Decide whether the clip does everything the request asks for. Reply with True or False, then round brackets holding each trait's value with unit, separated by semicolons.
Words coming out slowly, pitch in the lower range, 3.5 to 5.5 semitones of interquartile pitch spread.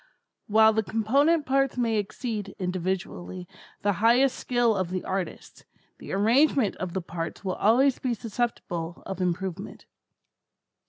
False (130 wpm; 210 Hz; 4.7 semitones)